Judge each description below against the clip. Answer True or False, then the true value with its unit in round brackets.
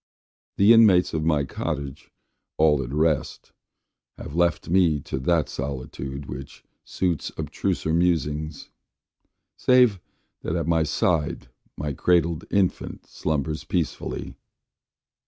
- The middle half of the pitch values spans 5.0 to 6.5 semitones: False (3.3 semitones)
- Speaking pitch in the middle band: False (80 Hz)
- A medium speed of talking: False (110 wpm)